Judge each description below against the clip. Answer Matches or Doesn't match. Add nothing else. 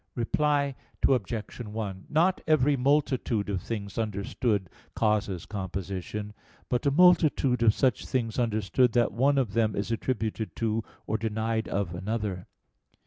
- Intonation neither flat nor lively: Matches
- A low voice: Matches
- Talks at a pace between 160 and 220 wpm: Doesn't match